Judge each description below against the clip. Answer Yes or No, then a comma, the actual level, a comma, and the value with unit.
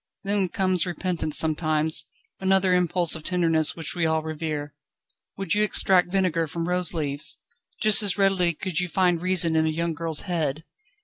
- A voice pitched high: No, medium, 170 Hz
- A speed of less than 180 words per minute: Yes, average, 170 wpm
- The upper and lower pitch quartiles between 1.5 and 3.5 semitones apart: Yes, average, 2.7 semitones